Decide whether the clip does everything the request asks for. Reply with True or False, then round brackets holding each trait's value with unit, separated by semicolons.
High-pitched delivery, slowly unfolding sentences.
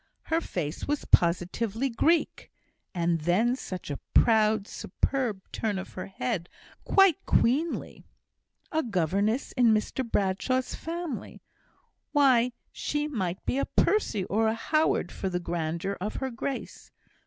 True (220 Hz; 130 wpm)